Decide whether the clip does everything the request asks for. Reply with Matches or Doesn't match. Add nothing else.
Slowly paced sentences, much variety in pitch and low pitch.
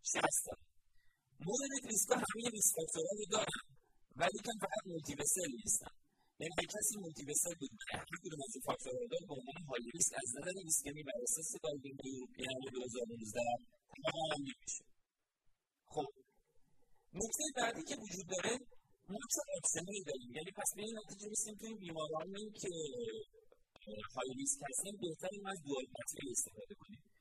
Doesn't match